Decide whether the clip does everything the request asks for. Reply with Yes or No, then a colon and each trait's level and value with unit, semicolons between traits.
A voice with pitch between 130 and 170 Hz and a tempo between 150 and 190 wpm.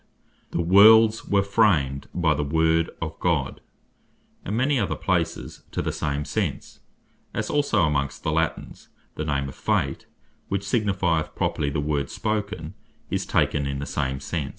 No: very low, 80 Hz; average, 160 wpm